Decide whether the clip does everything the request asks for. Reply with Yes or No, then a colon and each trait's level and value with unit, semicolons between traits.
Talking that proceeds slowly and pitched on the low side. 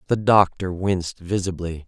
Yes: slow, 130 wpm; very low, 95 Hz